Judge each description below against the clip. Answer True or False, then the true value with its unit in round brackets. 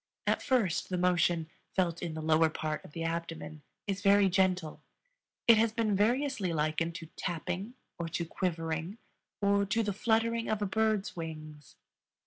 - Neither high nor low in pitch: True (180 Hz)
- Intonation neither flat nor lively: True (4.2 semitones)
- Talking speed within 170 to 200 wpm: False (160 wpm)